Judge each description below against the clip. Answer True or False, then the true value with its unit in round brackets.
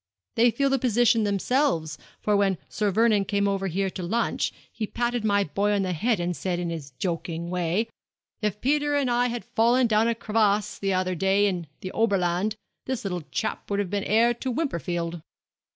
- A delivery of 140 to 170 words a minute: False (195 wpm)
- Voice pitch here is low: False (205 Hz)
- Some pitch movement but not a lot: True (4.3 semitones)